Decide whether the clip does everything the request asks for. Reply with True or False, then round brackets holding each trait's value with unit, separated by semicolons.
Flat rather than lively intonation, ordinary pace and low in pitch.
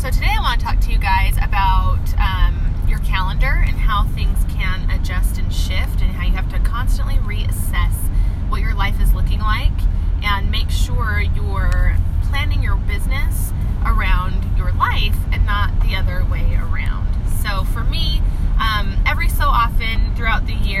True (2.2 semitones; 170 wpm; 90 Hz)